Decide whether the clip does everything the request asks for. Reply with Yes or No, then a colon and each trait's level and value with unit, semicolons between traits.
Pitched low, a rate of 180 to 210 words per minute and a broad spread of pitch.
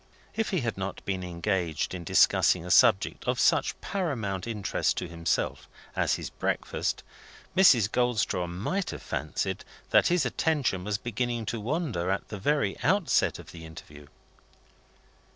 No: low, 105 Hz; average, 150 wpm; wide, 7.0 semitones